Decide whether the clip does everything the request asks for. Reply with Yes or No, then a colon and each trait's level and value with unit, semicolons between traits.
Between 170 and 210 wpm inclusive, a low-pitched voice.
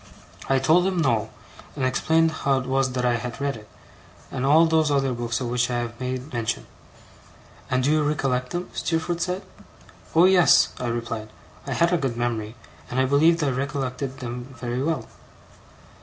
Yes: average, 185 wpm; low, 130 Hz